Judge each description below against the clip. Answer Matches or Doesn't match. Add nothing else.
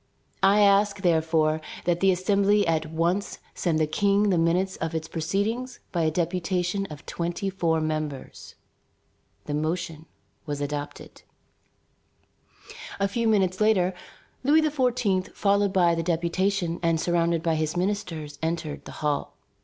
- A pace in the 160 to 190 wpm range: Doesn't match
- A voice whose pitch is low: Doesn't match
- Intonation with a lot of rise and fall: Doesn't match